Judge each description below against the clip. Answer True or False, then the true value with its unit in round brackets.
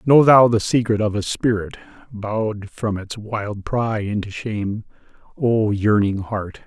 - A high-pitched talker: False (110 Hz)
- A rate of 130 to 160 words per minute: True (155 wpm)